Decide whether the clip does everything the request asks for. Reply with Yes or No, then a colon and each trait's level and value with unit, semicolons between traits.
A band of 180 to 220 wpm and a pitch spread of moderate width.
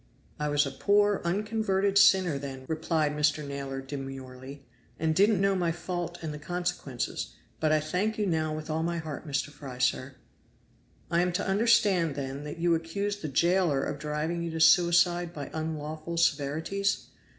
No: average, 170 wpm; average, 3.6 semitones